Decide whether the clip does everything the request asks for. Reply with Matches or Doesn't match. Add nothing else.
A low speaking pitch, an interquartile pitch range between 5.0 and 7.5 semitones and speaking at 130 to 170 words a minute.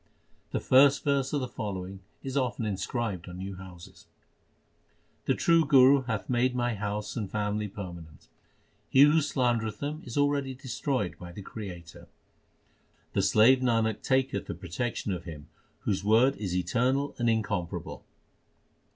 Matches